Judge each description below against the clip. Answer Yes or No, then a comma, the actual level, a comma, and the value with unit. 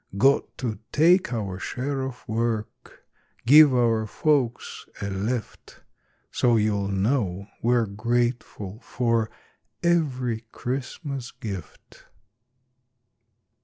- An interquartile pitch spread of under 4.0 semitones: Yes, average, 3.6 semitones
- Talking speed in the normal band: No, slow, 90 wpm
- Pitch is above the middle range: No, low, 120 Hz